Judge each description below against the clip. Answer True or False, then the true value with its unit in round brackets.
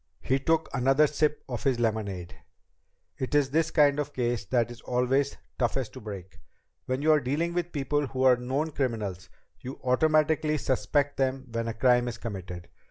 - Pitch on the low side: True (130 Hz)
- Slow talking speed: False (175 wpm)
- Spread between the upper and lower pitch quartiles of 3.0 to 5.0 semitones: True (3.7 semitones)